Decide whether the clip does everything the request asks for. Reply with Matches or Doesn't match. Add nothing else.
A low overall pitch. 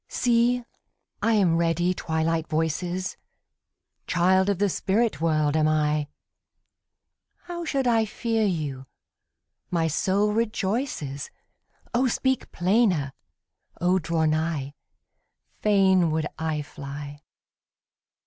Doesn't match